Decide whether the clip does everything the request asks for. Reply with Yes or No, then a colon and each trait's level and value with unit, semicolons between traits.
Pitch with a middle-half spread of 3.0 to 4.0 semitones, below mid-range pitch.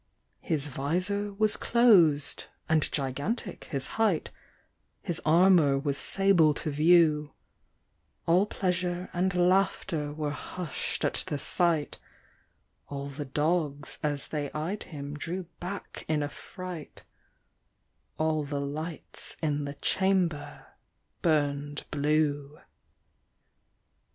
No: average, 3.7 semitones; medium, 155 Hz